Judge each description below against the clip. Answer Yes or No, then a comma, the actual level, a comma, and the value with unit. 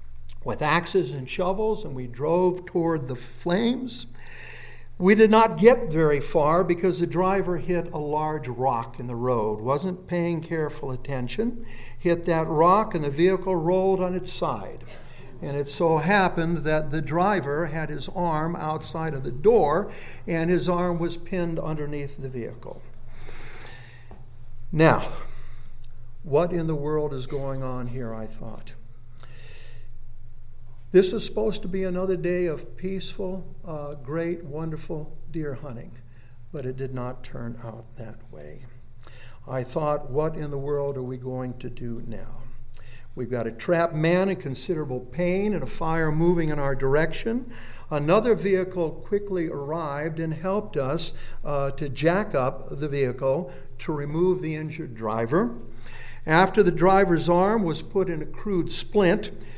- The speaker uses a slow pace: No, average, 150 wpm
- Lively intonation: Yes, wide, 6.0 semitones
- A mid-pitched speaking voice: Yes, medium, 155 Hz